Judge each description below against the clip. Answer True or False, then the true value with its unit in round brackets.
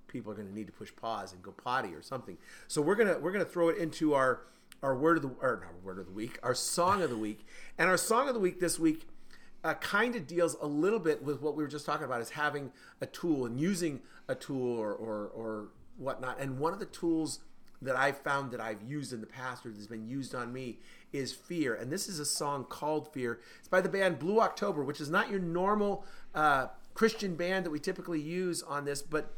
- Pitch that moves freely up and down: True (5.9 semitones)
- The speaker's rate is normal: False (250 wpm)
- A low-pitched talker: False (150 Hz)